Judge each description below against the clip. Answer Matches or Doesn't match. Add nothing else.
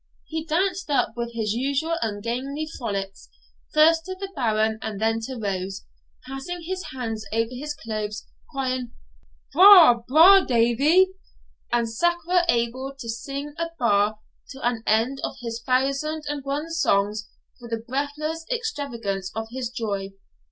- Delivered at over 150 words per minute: Doesn't match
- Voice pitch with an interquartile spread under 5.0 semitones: Doesn't match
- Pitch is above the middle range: Matches